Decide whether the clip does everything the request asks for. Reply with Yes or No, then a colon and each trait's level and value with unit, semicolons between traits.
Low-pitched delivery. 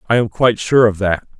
Yes: low, 110 Hz